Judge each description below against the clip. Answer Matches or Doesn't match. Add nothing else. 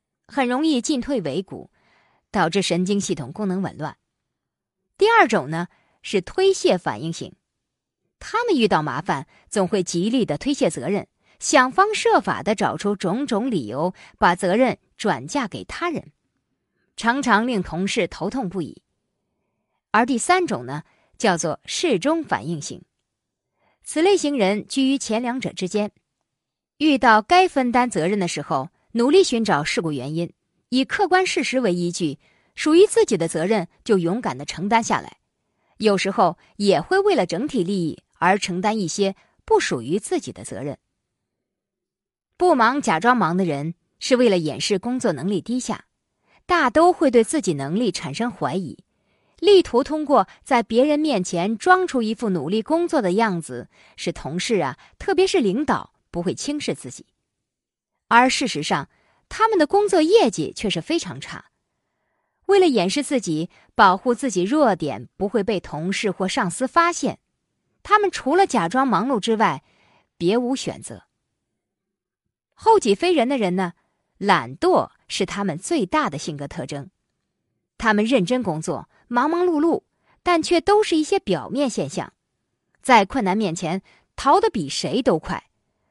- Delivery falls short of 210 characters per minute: Doesn't match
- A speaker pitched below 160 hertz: Doesn't match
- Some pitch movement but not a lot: Doesn't match